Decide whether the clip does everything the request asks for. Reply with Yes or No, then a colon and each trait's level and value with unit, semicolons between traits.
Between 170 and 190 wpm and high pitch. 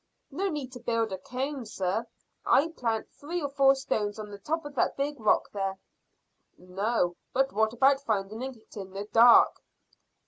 Yes: average, 180 wpm; high, 235 Hz